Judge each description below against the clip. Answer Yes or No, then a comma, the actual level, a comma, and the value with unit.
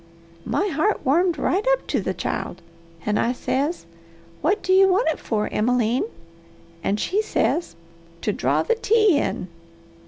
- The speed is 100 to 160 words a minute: Yes, average, 155 wpm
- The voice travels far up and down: Yes, wide, 8.4 semitones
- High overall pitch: Yes, very high, 325 Hz